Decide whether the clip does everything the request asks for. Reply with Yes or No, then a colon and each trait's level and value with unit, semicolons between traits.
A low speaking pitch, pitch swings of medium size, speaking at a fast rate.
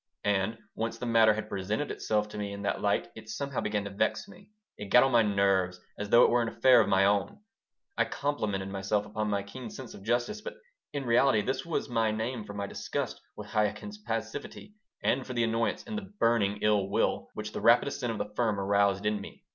Yes: low, 110 Hz; average, 3.0 semitones; fast, 225 wpm